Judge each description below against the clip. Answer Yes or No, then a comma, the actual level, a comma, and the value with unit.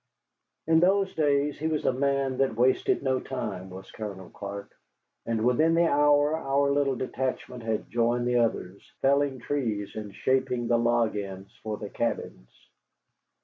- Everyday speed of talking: Yes, average, 155 wpm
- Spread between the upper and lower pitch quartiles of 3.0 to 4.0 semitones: No, average, 4.4 semitones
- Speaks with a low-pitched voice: Yes, low, 125 Hz